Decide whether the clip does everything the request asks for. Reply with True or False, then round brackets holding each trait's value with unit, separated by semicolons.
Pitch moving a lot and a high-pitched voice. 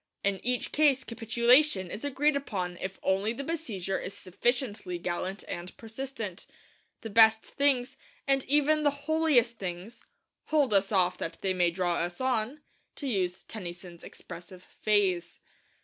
True (6.5 semitones; 220 Hz)